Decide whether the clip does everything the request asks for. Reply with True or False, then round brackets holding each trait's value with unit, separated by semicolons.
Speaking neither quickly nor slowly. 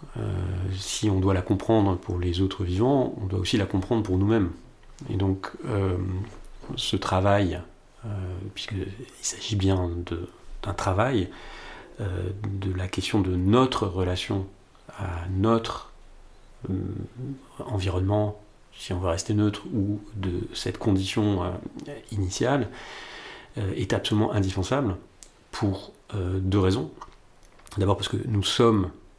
False (130 wpm)